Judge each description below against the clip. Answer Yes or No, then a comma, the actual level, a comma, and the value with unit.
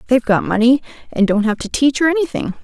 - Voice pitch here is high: Yes, very high, 250 Hz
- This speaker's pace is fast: Yes, fast, 230 wpm